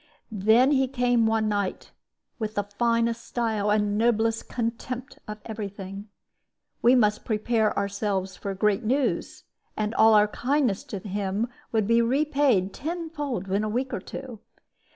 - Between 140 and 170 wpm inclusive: Yes, average, 150 wpm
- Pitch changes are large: No, average, 3.0 semitones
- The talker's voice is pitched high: Yes, high, 220 Hz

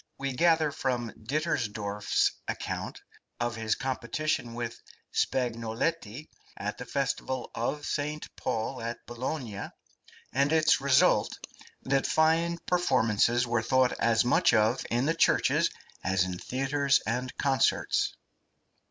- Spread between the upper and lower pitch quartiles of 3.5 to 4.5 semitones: Yes, average, 3.9 semitones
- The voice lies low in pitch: Yes, low, 125 Hz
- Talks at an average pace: No, slow, 115 wpm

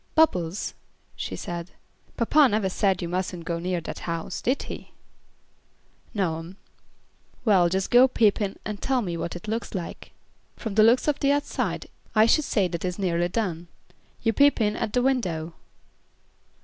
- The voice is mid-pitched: No, high, 195 Hz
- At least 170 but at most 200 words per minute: Yes, average, 175 wpm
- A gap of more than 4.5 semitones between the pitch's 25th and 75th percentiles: Yes, average, 4.9 semitones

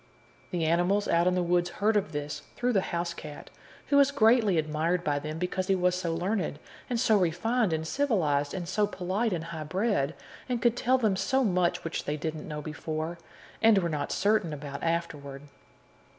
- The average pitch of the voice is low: No, medium, 175 Hz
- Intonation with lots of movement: No, average, 4.7 semitones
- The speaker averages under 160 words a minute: No, average, 190 wpm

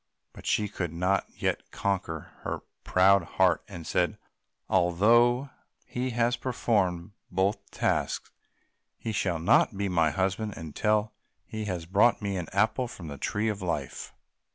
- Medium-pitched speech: No, low, 100 Hz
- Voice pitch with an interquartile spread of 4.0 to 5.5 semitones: No, average, 3.6 semitones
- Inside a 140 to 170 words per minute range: Yes, average, 150 wpm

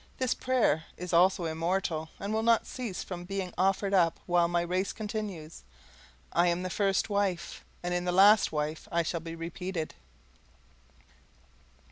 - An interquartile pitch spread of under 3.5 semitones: Yes, average, 2.7 semitones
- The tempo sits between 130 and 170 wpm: Yes, average, 155 wpm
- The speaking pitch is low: No, medium, 180 Hz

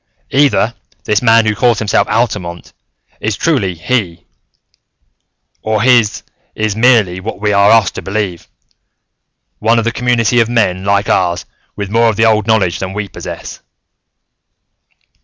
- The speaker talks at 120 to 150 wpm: Yes, average, 145 wpm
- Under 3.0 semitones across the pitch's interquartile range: Yes, narrow, 2.6 semitones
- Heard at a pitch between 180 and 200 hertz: No, low, 110 Hz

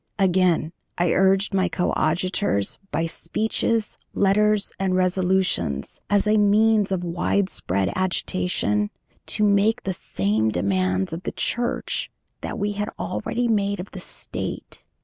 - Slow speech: Yes, slow, 130 wpm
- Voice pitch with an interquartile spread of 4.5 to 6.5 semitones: No, average, 3.4 semitones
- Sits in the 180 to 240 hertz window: Yes, high, 190 Hz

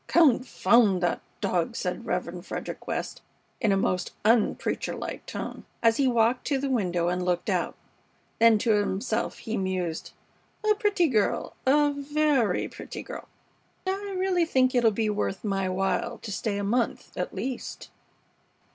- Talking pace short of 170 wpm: Yes, average, 155 wpm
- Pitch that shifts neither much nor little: No, wide, 6.0 semitones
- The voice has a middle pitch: No, high, 230 Hz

